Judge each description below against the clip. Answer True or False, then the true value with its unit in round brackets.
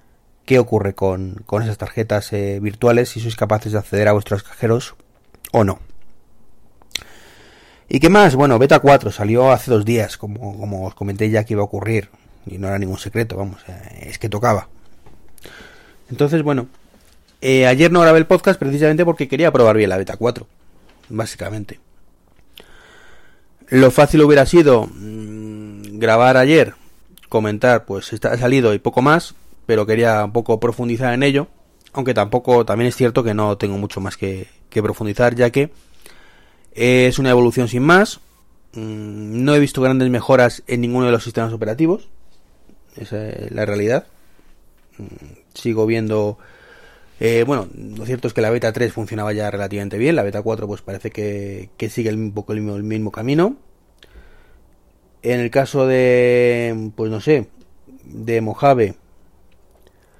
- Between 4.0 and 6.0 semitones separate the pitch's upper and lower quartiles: False (3.5 semitones)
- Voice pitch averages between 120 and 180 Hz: False (110 Hz)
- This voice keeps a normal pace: True (155 wpm)